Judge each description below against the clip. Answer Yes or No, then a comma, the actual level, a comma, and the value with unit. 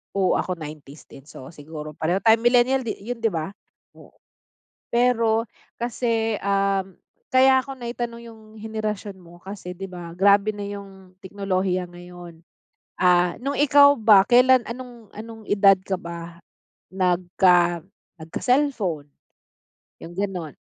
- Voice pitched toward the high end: Yes, high, 195 Hz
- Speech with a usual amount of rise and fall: Yes, average, 4.6 semitones